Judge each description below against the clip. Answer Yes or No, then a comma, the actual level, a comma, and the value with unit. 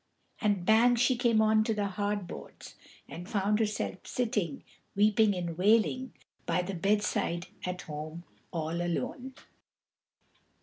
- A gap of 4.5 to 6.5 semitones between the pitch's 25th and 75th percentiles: No, average, 4.0 semitones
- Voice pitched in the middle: No, high, 205 Hz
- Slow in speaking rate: Yes, slow, 130 wpm